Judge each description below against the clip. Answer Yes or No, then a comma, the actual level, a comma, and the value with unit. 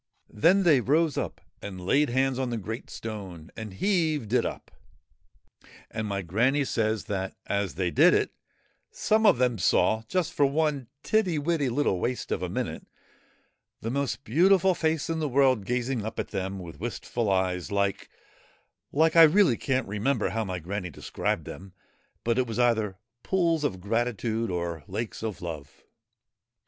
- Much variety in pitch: Yes, wide, 6.5 semitones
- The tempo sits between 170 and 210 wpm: Yes, average, 175 wpm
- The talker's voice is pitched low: Yes, low, 120 Hz